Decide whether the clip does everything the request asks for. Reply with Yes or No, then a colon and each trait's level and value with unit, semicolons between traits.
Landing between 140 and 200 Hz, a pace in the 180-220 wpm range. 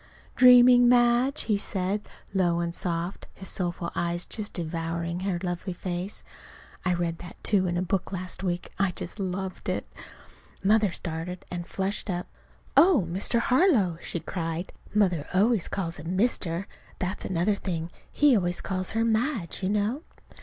No: medium, 185 Hz; average, 155 wpm